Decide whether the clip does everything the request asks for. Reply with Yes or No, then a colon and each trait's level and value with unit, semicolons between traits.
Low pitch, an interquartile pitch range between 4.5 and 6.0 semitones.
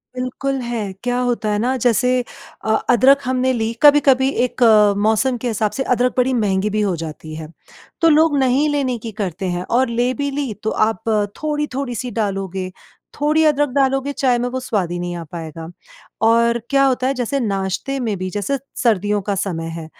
No: high, 240 Hz; average, 4.8 semitones